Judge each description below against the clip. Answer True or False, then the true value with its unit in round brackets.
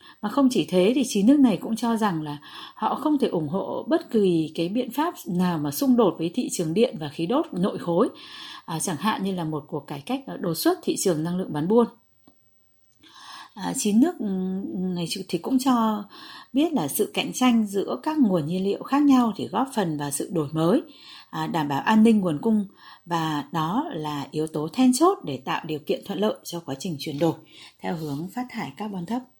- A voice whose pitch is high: True (205 Hz)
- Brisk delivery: False (220 wpm)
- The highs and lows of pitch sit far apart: True (7.7 semitones)